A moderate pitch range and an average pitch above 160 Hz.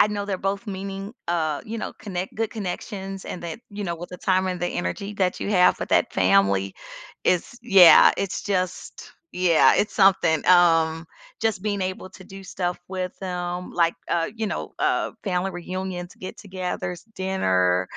No: narrow, 2.0 semitones; medium, 185 Hz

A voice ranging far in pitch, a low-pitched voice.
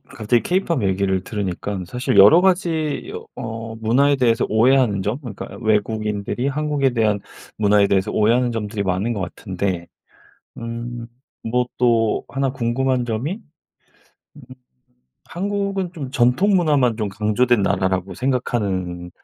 No: average, 4.5 semitones; low, 115 Hz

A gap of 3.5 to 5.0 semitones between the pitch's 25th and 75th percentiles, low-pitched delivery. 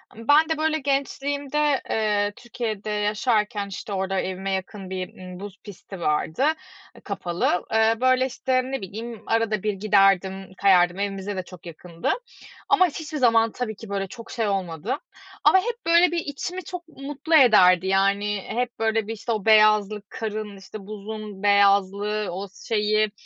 No: average, 4.2 semitones; high, 210 Hz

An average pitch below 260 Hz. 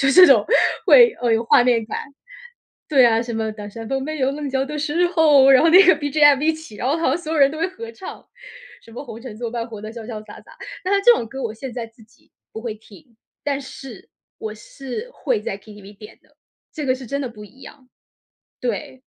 No: very high, 265 Hz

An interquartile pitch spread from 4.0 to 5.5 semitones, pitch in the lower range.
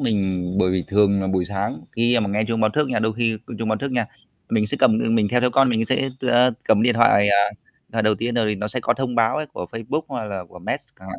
No: average, 3.0 semitones; low, 110 Hz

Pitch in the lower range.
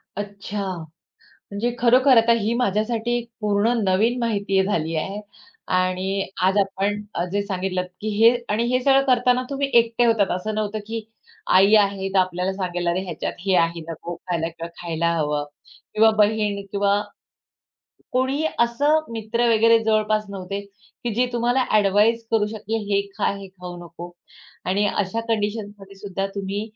No: high, 205 Hz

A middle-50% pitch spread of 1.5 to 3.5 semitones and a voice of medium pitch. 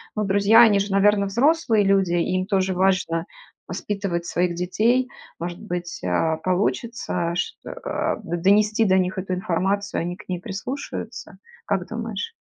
No: average, 2.9 semitones; high, 195 Hz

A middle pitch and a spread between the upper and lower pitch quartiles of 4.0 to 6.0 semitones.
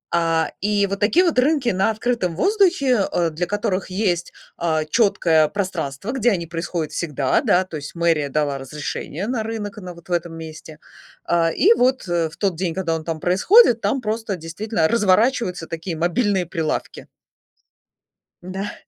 Yes: medium, 180 Hz; average, 4.8 semitones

